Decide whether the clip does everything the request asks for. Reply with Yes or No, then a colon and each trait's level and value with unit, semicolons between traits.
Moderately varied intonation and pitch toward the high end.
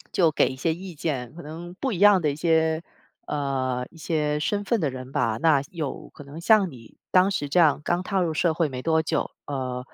No: average, 4.0 semitones; medium, 160 Hz